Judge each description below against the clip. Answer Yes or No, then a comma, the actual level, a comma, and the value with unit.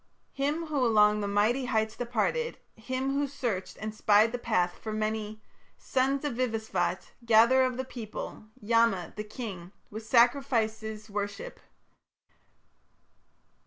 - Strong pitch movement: No, average, 3.2 semitones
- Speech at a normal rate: No, slow, 125 wpm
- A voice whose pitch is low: No, high, 225 Hz